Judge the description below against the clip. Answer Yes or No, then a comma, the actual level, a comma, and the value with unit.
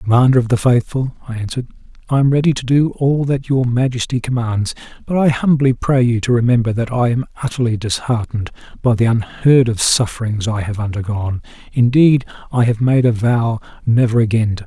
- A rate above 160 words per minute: Yes, average, 190 wpm